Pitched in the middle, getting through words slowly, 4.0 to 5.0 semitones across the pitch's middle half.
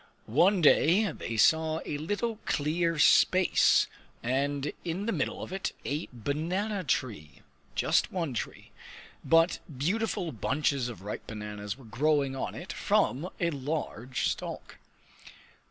No: medium, 150 Hz; slow, 130 wpm; wide, 5.5 semitones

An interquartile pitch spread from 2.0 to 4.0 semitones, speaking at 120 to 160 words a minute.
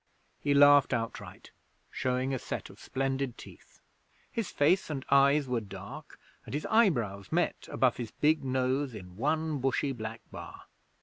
Yes: average, 3.5 semitones; average, 150 wpm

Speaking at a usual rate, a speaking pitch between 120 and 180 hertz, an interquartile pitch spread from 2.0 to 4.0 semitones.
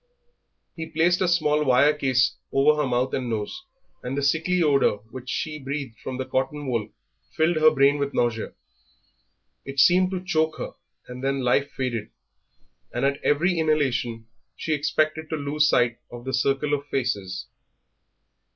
Yes: average, 160 wpm; medium, 140 Hz; average, 3.4 semitones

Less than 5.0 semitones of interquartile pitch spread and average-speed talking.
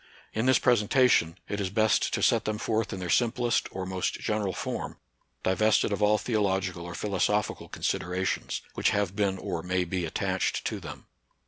Yes: average, 2.8 semitones; average, 180 wpm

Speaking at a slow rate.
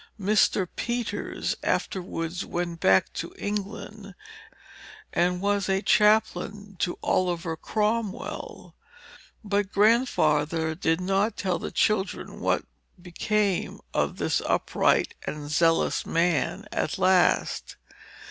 Yes: slow, 100 wpm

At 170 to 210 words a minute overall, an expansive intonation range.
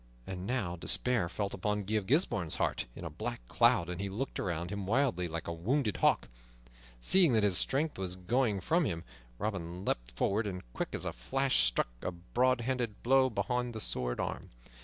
Yes: average, 195 wpm; wide, 5.8 semitones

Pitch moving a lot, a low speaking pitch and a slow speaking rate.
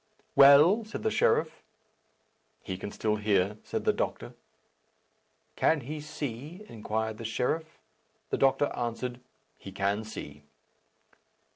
Yes: wide, 6.2 semitones; low, 120 Hz; slow, 120 wpm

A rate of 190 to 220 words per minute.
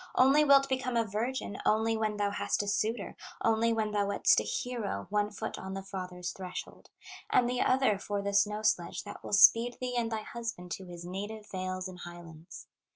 Yes: average, 200 wpm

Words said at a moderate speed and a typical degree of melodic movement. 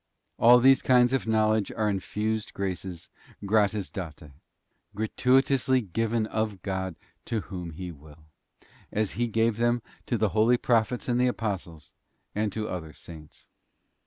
Yes: average, 150 wpm; average, 3.9 semitones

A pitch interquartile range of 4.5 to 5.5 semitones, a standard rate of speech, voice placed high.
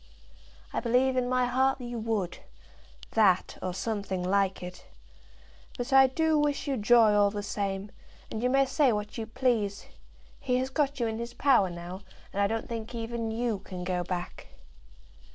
No: average, 4.1 semitones; average, 175 wpm; high, 225 Hz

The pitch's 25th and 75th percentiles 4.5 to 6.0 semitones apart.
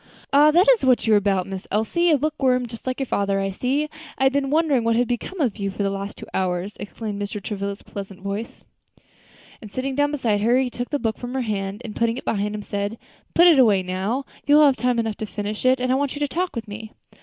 Yes: average, 4.8 semitones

